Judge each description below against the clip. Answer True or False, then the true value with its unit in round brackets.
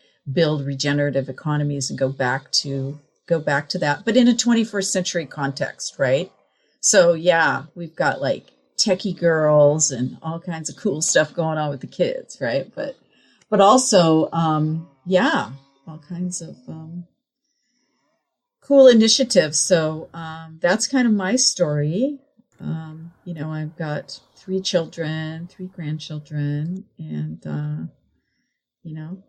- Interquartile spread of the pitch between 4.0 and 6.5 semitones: True (4.3 semitones)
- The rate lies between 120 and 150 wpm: True (140 wpm)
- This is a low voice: False (165 Hz)